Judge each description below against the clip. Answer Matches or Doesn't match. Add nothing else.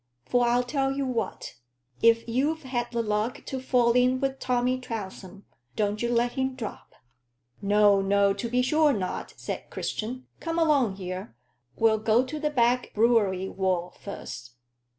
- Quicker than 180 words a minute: Doesn't match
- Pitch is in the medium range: Doesn't match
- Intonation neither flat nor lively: Matches